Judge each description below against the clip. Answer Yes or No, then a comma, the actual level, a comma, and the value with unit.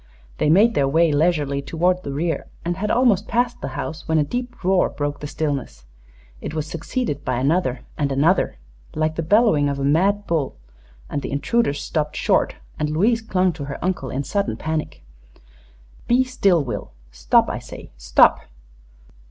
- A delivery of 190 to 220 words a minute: No, average, 175 wpm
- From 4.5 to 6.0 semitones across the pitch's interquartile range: Yes, average, 5.1 semitones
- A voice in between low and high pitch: Yes, medium, 160 Hz